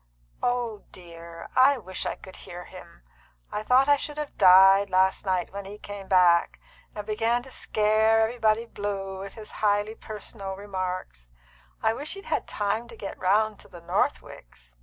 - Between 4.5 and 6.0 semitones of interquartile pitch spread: No, average, 3.1 semitones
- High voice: Yes, high, 205 Hz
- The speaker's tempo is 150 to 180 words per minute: Yes, average, 170 wpm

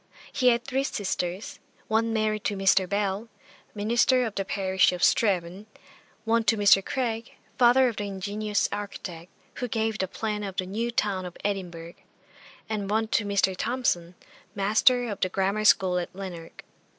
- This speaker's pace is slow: No, average, 160 wpm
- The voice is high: Yes, high, 205 Hz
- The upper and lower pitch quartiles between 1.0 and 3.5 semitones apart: Yes, average, 2.9 semitones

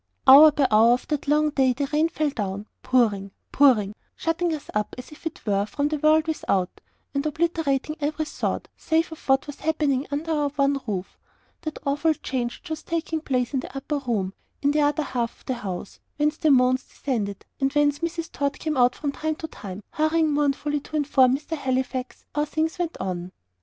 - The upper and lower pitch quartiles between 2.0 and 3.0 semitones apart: No, average, 3.6 semitones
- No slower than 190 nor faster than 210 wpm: Yes, average, 200 wpm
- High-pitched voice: Yes, very high, 285 Hz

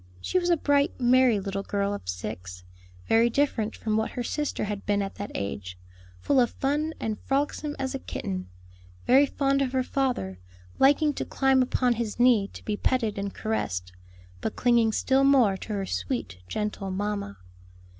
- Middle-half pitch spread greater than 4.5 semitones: Yes, average, 5.2 semitones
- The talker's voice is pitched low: No, high, 225 Hz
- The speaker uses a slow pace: No, average, 175 wpm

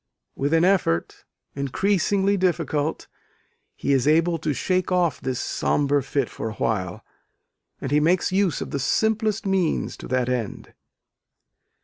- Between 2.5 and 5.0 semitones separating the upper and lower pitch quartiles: No, wide, 5.6 semitones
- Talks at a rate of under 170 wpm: Yes, slow, 135 wpm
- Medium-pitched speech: Yes, medium, 155 Hz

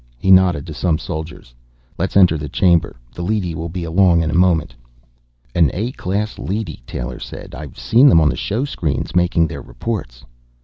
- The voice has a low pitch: Yes, very low, 85 Hz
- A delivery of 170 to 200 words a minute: Yes, average, 180 wpm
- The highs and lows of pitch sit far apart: No, average, 3.4 semitones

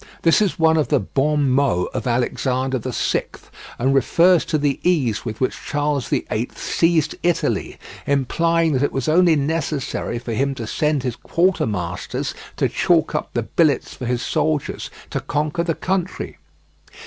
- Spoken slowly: No, average, 160 wpm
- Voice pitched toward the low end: No, medium, 145 Hz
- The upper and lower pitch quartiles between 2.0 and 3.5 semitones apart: No, average, 4.2 semitones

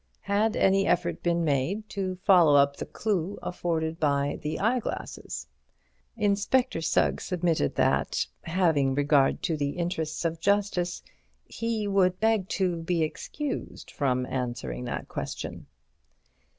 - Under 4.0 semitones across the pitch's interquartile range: No, average, 4.6 semitones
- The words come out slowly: Yes, slow, 125 wpm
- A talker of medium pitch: Yes, medium, 175 Hz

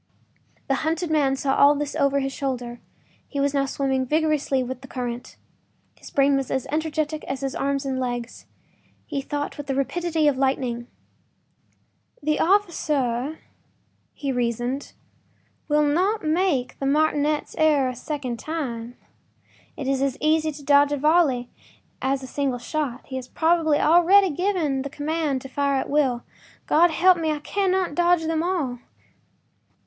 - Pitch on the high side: Yes, very high, 285 Hz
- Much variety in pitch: No, average, 2.9 semitones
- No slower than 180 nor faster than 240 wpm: No, average, 155 wpm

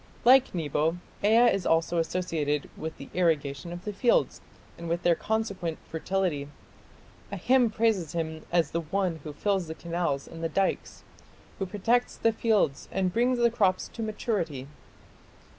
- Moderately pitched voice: Yes, medium, 175 Hz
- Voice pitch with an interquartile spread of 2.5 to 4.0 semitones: No, average, 4.9 semitones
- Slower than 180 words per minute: Yes, average, 160 wpm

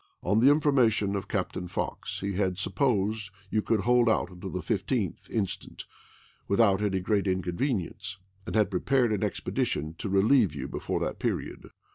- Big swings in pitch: No, average, 3.2 semitones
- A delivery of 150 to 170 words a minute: Yes, average, 160 wpm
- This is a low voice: Yes, low, 100 Hz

